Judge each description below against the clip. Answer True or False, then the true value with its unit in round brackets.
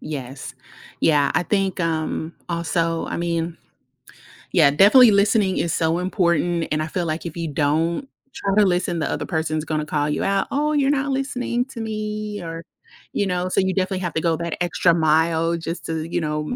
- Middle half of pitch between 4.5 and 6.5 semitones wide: False (3.6 semitones)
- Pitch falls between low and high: True (170 Hz)